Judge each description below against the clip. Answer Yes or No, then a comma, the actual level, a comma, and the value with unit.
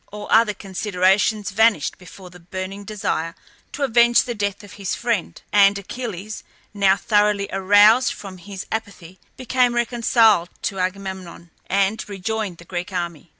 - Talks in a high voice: Yes, high, 200 Hz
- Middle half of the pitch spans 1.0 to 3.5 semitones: Yes, average, 2.8 semitones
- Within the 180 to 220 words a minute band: No, average, 145 wpm